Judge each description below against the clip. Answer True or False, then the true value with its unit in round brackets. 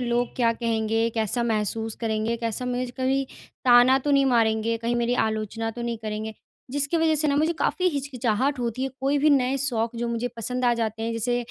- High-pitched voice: True (240 Hz)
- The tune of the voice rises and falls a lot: False (2.7 semitones)